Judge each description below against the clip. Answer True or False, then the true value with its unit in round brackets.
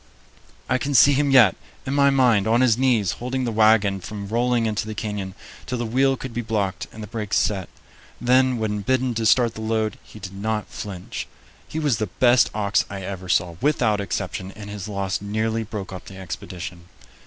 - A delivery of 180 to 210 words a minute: True (200 wpm)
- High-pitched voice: False (110 Hz)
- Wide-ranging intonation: False (3.7 semitones)